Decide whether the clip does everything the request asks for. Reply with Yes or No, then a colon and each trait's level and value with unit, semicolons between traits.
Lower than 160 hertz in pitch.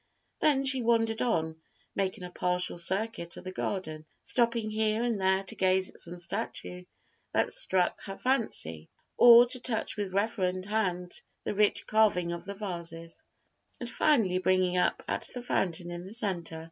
No: high, 190 Hz